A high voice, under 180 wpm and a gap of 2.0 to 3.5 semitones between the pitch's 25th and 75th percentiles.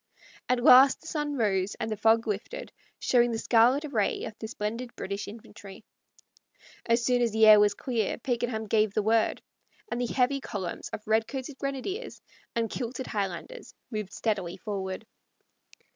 Yes: high, 225 Hz; average, 160 wpm; average, 3.0 semitones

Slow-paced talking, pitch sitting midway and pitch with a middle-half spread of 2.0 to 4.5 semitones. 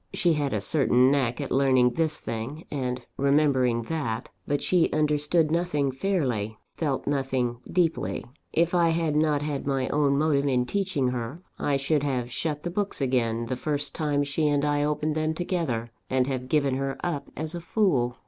No: average, 180 wpm; medium, 145 Hz; average, 3.5 semitones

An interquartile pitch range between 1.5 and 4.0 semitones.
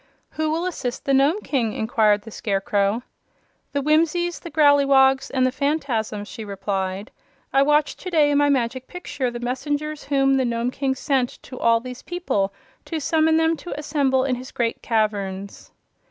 No: average, 4.5 semitones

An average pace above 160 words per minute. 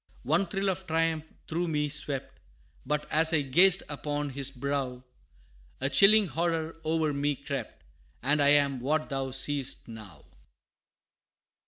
No: average, 140 wpm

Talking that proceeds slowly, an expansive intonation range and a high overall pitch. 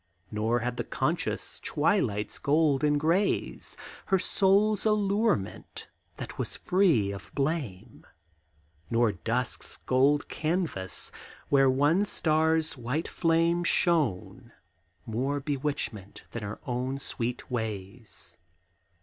No: slow, 105 wpm; wide, 6.1 semitones; medium, 140 Hz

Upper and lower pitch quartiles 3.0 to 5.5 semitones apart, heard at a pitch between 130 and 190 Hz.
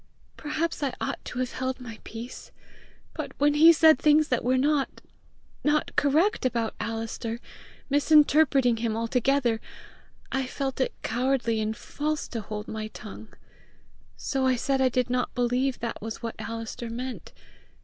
No: average, 3.8 semitones; very high, 255 Hz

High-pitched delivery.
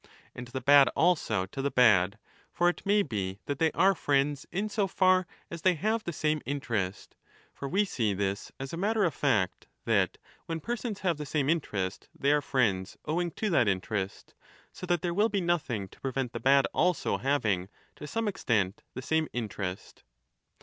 No: medium, 145 Hz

